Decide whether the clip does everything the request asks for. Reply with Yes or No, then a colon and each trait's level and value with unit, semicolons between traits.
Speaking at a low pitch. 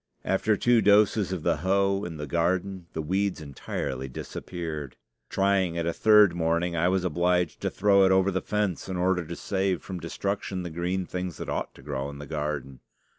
Yes: very low, 90 Hz